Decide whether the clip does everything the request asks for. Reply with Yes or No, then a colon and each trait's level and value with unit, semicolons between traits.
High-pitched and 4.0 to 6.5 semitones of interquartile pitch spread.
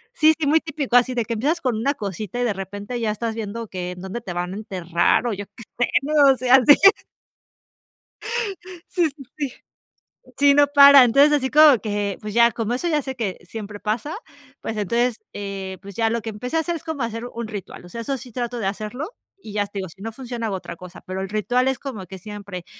Yes: high, 230 Hz; average, 4.6 semitones